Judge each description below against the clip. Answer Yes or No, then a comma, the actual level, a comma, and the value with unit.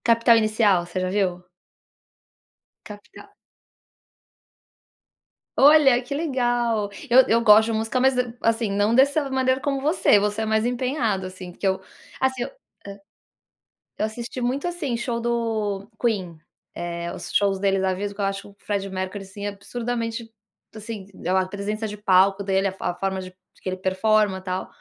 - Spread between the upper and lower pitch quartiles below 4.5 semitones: Yes, average, 3.8 semitones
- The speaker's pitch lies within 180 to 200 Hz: No, high, 215 Hz